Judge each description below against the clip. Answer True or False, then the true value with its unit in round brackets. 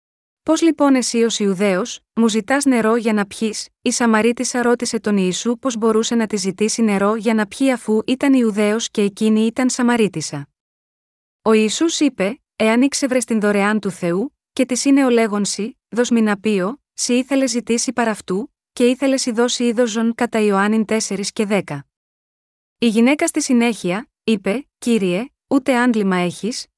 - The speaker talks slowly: False (160 wpm)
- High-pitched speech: True (230 Hz)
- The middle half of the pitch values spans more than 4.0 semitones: False (3.0 semitones)